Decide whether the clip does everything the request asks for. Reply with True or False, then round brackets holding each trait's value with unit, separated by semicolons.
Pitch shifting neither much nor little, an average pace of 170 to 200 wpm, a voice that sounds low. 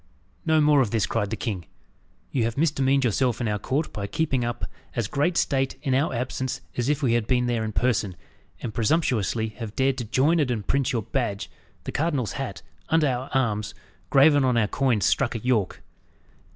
True (3.6 semitones; 195 wpm; 125 Hz)